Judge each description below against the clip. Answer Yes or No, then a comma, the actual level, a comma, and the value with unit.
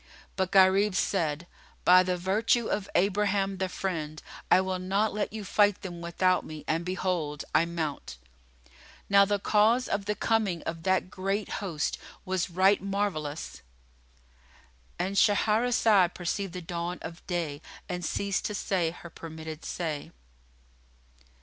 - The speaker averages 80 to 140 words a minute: Yes, slow, 135 wpm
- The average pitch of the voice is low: No, medium, 185 Hz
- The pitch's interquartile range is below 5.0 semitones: Yes, average, 3.4 semitones